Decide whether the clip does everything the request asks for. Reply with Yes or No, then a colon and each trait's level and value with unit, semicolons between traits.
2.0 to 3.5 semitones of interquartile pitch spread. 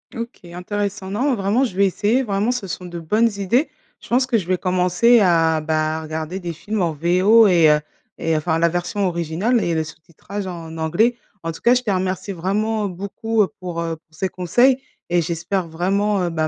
No: average, 4.1 semitones